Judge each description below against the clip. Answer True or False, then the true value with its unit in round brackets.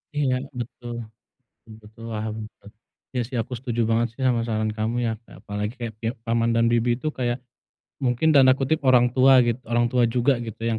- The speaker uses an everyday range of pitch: False (2.1 semitones)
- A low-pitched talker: True (120 Hz)